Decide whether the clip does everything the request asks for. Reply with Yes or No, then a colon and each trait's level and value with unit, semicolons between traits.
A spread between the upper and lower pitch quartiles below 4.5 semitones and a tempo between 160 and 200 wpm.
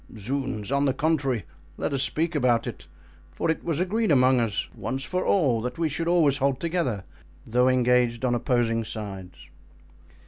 No: average, 4.8 semitones; average, 170 wpm